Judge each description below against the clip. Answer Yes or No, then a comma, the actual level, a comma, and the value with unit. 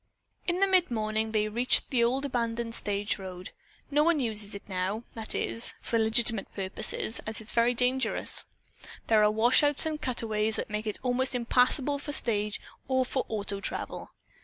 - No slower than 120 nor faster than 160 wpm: No, average, 175 wpm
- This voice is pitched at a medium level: No, high, 230 Hz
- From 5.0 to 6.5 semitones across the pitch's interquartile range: No, average, 3.2 semitones